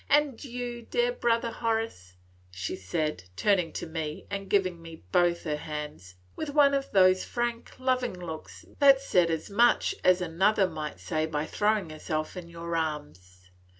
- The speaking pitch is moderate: Yes, medium, 180 Hz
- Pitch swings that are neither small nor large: No, wide, 7.0 semitones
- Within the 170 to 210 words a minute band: No, average, 160 wpm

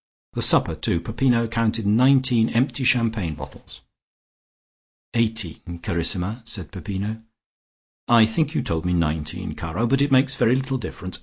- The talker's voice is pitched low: Yes, low, 110 Hz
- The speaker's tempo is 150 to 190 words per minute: No, average, 140 wpm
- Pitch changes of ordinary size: No, wide, 5.9 semitones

